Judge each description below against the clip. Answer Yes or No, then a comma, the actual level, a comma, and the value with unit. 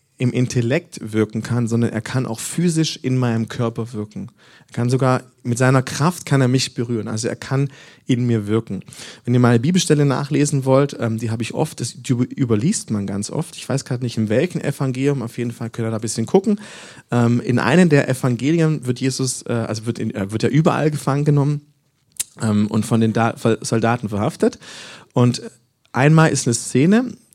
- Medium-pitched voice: No, low, 125 Hz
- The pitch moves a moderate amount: Yes, average, 3.8 semitones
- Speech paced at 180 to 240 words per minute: Yes, average, 185 wpm